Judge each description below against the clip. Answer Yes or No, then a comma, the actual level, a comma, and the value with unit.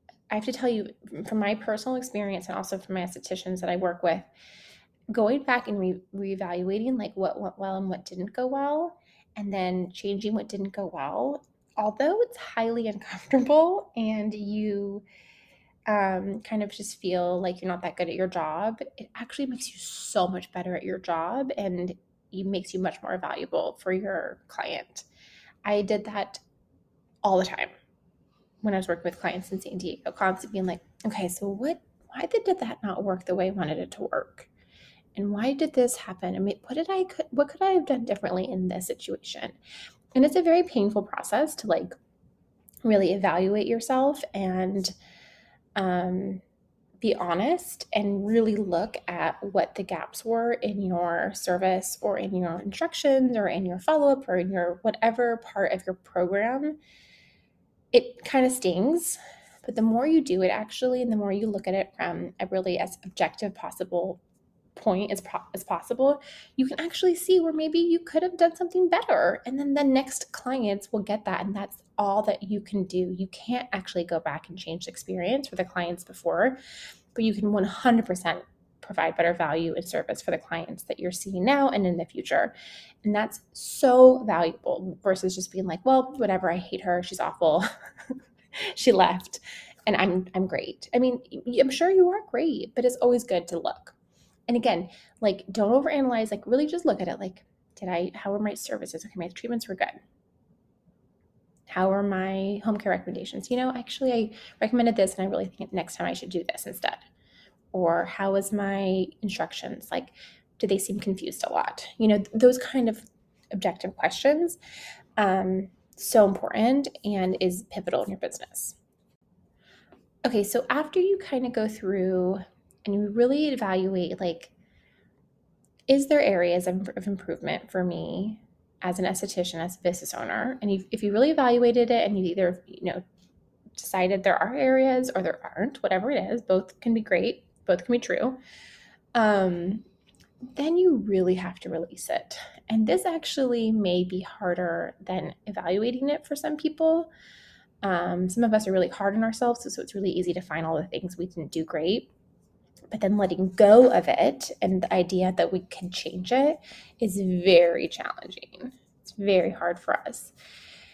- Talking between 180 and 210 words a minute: Yes, average, 185 wpm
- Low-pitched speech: No, high, 205 Hz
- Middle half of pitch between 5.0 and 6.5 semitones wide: Yes, average, 5.3 semitones